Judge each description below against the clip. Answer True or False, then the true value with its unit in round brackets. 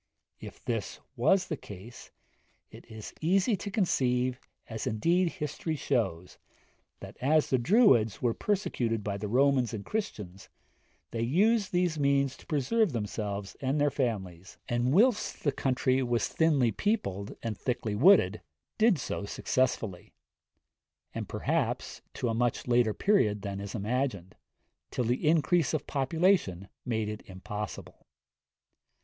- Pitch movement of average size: False (7.0 semitones)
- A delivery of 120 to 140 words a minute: True (135 wpm)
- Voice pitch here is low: True (125 Hz)